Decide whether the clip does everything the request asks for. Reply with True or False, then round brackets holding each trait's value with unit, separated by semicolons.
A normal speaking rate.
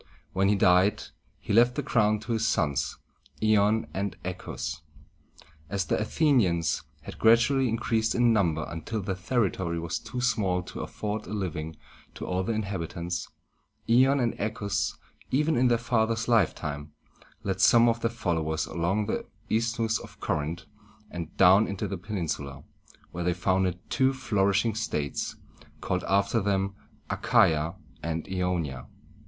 True (155 wpm)